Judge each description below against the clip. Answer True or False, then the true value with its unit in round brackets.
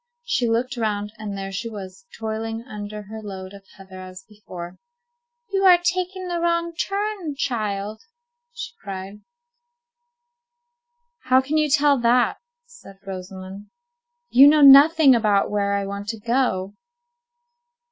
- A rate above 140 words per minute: False (135 wpm)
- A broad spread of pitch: True (6.6 semitones)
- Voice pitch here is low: False (220 Hz)